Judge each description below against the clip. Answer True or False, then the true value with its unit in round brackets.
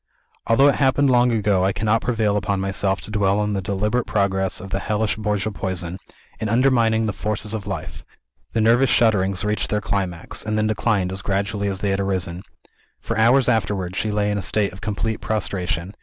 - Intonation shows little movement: True (2.3 semitones)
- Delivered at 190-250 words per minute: True (200 wpm)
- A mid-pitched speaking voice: False (105 Hz)